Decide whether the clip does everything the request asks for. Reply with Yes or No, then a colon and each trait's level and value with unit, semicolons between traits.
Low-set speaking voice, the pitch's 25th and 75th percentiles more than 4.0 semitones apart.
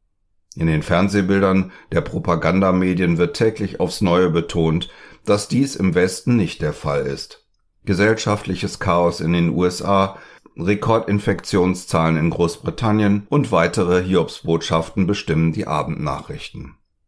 No: very low, 95 Hz; average, 3.0 semitones